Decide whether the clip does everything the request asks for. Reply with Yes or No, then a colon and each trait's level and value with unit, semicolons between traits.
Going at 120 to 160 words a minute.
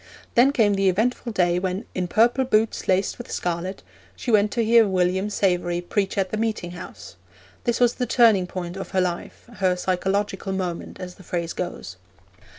No: average, 180 wpm